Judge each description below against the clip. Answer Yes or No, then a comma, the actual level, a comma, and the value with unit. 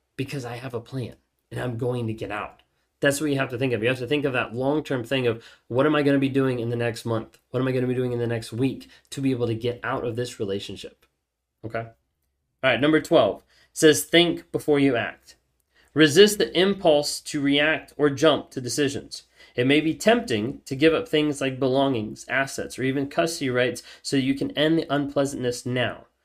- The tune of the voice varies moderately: Yes, average, 3.7 semitones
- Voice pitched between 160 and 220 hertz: No, low, 135 Hz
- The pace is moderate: No, fast, 230 wpm